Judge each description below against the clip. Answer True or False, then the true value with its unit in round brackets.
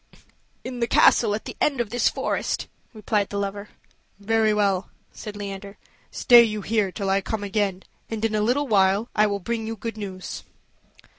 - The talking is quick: False (180 wpm)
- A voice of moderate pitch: False (210 Hz)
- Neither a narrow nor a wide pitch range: False (2.1 semitones)